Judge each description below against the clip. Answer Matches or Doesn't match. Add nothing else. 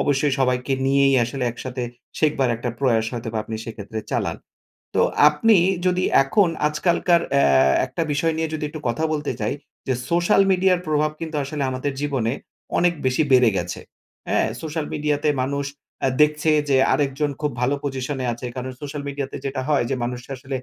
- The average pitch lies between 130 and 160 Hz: Matches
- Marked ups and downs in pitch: Doesn't match